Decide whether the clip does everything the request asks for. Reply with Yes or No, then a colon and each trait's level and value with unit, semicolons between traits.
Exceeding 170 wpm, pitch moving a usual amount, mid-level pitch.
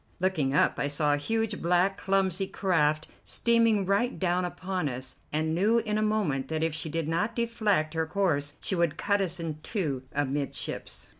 Yes: average, 180 wpm; average, 4.7 semitones; medium, 175 Hz